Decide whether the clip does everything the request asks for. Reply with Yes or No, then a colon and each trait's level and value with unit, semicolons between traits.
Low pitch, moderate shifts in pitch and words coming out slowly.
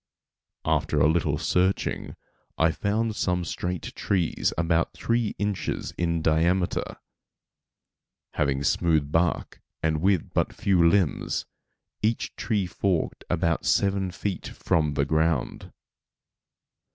Yes: very low, 85 Hz; average, 3.4 semitones; slow, 110 wpm